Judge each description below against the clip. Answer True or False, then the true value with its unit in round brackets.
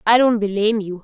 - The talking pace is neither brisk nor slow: False (230 wpm)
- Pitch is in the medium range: False (215 Hz)